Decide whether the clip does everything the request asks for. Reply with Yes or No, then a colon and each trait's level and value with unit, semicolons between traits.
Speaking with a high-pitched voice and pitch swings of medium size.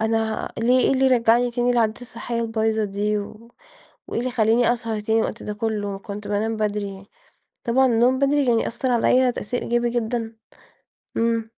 No: high, 230 Hz; narrow, 2.0 semitones